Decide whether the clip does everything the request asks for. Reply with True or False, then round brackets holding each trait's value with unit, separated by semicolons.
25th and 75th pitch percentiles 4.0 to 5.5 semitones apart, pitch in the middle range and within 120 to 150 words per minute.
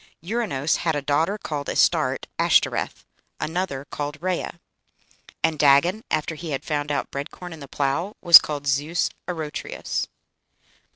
False (3.2 semitones; 155 Hz; 140 wpm)